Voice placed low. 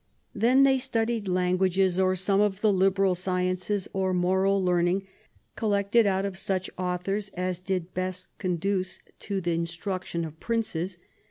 No: high, 190 Hz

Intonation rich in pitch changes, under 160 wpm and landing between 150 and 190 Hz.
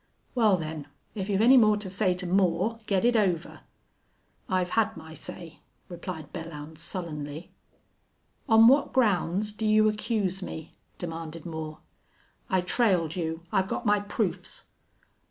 No: average, 4.4 semitones; average, 140 wpm; medium, 185 Hz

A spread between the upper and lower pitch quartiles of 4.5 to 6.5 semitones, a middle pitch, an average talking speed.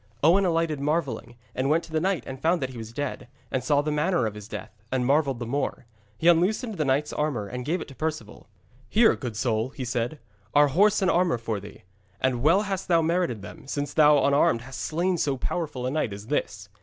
No: average, 5.2 semitones; medium, 145 Hz; fast, 225 wpm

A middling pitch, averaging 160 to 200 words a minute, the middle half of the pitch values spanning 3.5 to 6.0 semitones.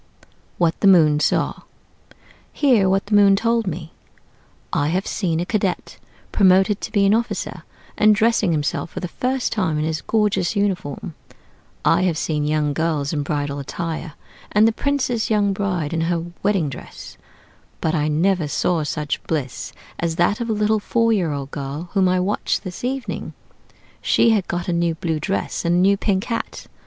Yes: medium, 180 Hz; average, 180 wpm; average, 4.6 semitones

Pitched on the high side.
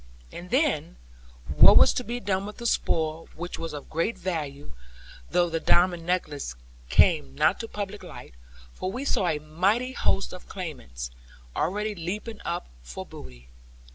No: medium, 175 Hz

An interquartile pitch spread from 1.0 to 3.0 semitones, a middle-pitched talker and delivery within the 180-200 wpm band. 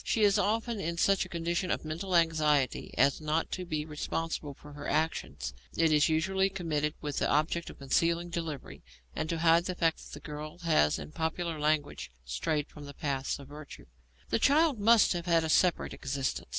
Yes: narrow, 2.6 semitones; medium, 160 Hz; average, 195 wpm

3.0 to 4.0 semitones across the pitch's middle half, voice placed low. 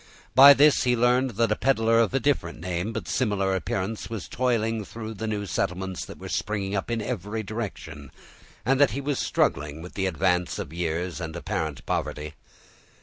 No: average, 4.8 semitones; low, 105 Hz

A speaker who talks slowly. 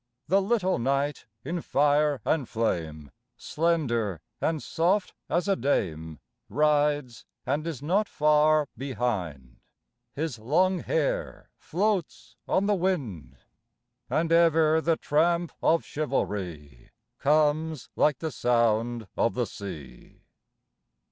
Yes: slow, 110 wpm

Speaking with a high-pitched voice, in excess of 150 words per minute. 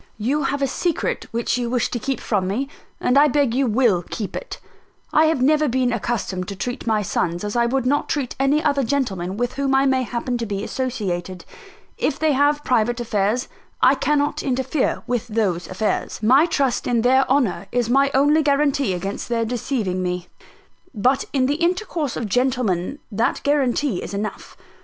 Yes: very high, 250 Hz; average, 185 wpm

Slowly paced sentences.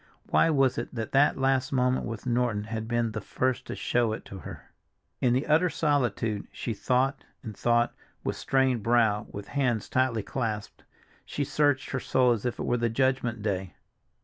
No: average, 185 wpm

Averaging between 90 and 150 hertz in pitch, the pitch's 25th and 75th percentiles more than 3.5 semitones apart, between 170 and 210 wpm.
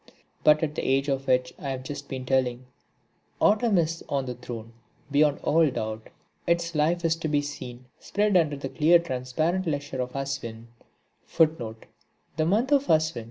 No: medium, 140 Hz; average, 4.2 semitones; average, 150 wpm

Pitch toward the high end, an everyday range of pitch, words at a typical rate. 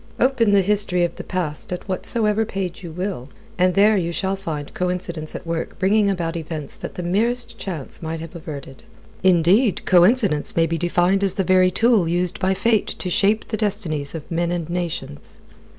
No: medium, 180 Hz; average, 3.1 semitones; average, 185 wpm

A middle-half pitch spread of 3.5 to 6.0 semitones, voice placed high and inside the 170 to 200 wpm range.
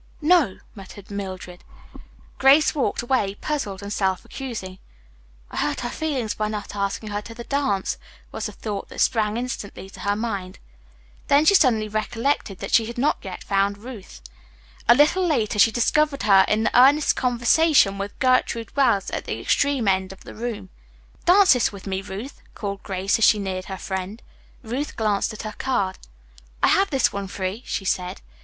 Yes: average, 4.8 semitones; high, 215 Hz; average, 175 wpm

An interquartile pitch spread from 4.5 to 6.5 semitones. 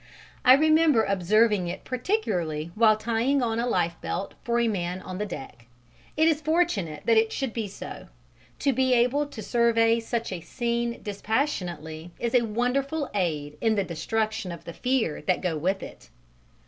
Yes: average, 5.3 semitones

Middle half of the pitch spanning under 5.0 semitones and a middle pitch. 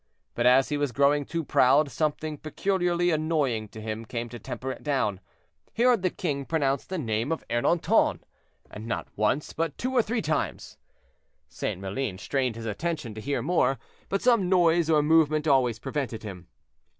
No: wide, 5.6 semitones; medium, 145 Hz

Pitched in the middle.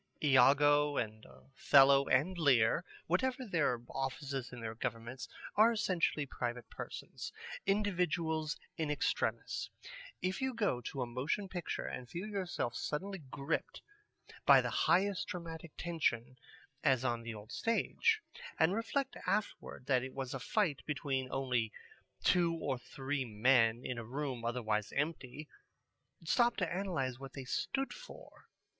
Yes: medium, 145 Hz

